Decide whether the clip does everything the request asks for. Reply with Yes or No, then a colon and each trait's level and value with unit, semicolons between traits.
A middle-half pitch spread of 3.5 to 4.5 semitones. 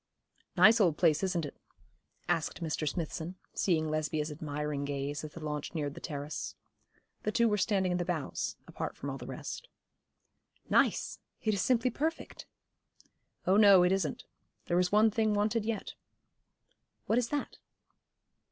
No: wide, 5.6 semitones